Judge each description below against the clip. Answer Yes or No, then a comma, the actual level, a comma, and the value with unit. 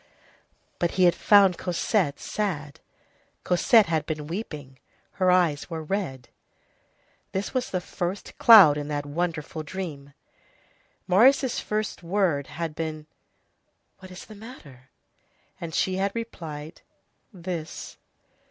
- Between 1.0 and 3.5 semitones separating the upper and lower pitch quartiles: No, average, 4.4 semitones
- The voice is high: No, medium, 175 Hz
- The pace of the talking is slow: Yes, slow, 120 wpm